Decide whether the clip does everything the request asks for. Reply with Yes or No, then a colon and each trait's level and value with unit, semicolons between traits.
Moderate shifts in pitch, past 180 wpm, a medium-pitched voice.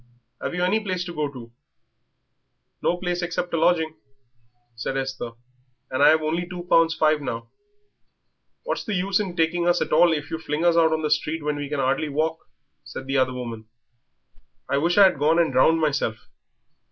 Yes: average, 3.7 semitones; average, 195 wpm; medium, 160 Hz